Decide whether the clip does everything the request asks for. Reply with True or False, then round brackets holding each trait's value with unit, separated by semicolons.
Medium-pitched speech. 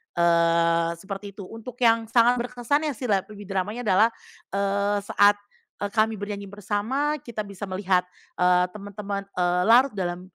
False (205 Hz)